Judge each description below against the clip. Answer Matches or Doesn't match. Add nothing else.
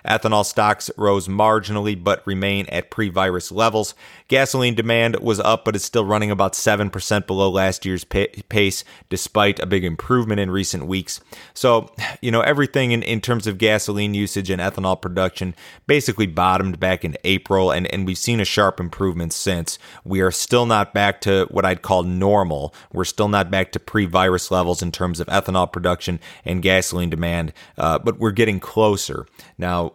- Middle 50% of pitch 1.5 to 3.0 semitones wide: Matches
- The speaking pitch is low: Matches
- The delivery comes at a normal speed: Matches